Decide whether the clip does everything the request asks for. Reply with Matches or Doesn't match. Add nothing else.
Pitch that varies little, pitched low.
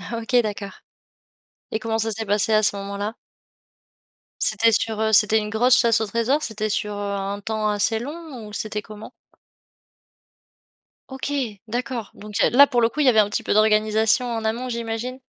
Doesn't match